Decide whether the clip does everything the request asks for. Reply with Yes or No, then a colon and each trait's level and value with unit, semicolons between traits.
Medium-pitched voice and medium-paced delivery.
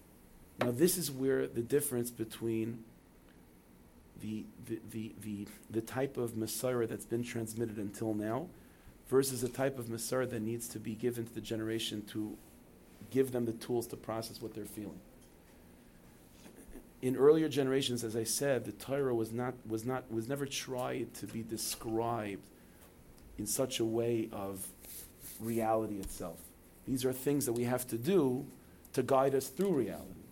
No: low, 115 Hz; average, 160 wpm